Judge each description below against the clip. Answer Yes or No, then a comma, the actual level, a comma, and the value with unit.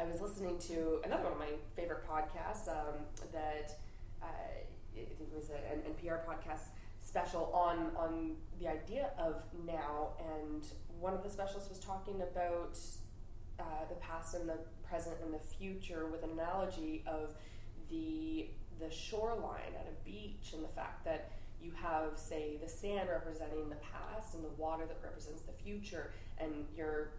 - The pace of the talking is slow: No, average, 170 wpm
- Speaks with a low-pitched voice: No, medium, 160 Hz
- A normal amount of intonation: No, narrow, 2.3 semitones